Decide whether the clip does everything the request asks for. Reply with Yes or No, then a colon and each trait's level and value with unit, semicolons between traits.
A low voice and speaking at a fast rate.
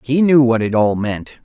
Yes: low, 125 Hz; fast, 250 wpm